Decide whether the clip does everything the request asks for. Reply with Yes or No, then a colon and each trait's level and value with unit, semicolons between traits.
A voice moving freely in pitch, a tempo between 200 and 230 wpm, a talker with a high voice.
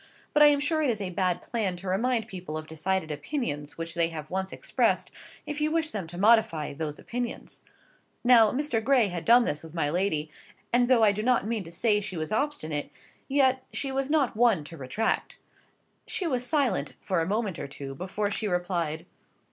Yes: wide, 7.0 semitones; fast, 205 wpm; high, 200 Hz